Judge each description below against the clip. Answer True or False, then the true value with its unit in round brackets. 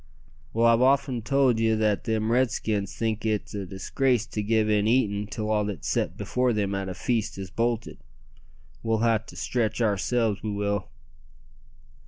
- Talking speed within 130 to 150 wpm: False (170 wpm)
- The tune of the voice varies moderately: False (2.3 semitones)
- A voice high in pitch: False (110 Hz)